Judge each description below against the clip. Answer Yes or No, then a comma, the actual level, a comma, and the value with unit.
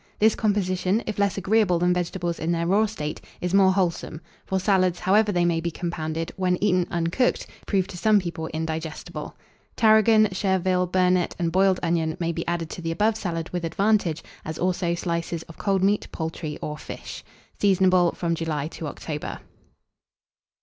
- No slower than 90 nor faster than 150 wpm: No, average, 170 wpm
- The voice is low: No, medium, 180 Hz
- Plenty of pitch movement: No, average, 2.7 semitones